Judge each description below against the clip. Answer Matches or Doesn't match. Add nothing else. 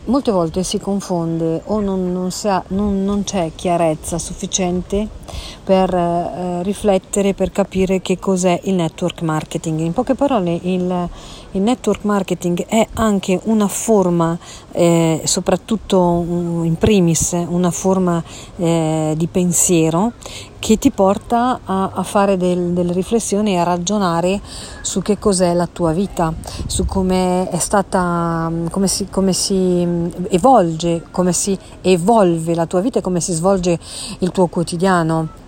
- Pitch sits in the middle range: Matches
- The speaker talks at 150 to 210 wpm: Doesn't match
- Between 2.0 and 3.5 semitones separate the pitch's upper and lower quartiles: Matches